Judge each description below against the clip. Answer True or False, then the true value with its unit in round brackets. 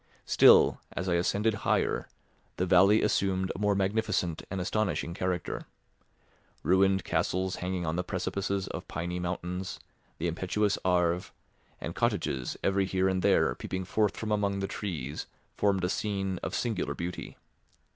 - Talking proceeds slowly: False (145 wpm)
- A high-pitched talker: False (95 Hz)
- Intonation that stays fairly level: True (2.0 semitones)